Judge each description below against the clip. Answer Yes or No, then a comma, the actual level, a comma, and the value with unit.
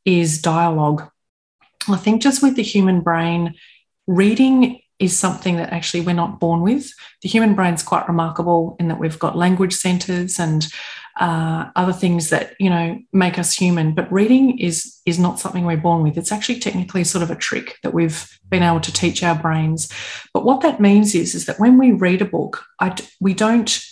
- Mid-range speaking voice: Yes, medium, 180 Hz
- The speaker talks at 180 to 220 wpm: Yes, average, 195 wpm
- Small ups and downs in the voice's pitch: No, average, 3.7 semitones